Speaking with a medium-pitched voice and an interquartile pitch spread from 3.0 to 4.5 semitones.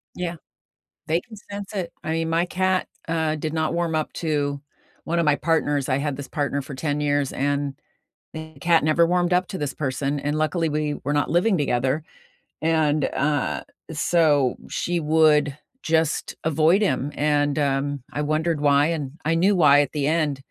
No: medium, 155 Hz; narrow, 2.5 semitones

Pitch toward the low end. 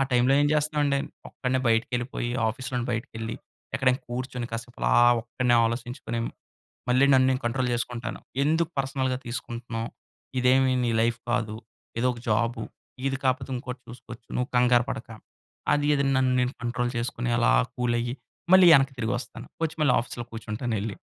Yes: low, 125 Hz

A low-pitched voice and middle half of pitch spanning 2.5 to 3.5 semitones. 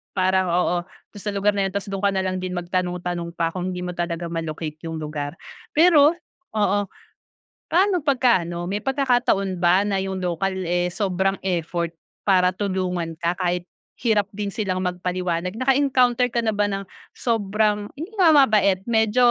No: high, 190 Hz; average, 3.2 semitones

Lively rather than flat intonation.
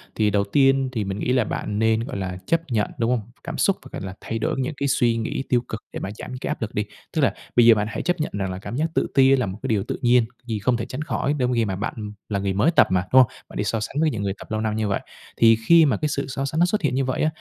No: average, 4.4 semitones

